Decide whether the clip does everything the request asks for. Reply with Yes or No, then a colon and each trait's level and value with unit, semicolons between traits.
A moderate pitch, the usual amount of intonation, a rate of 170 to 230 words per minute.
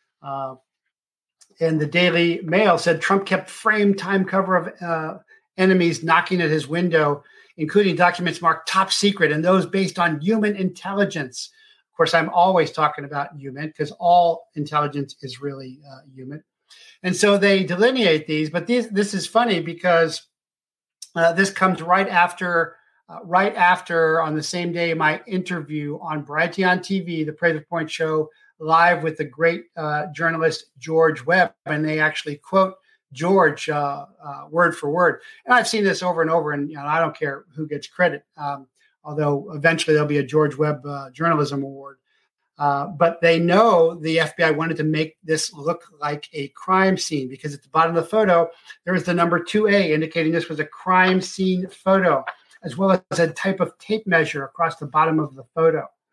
Yes: medium, 165 Hz; average, 3.3 semitones; average, 180 wpm